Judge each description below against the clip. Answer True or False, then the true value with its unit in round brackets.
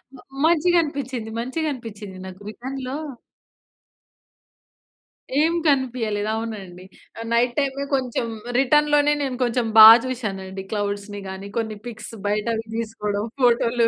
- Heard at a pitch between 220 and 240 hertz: True (230 Hz)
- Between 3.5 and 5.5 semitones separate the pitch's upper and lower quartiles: True (4.0 semitones)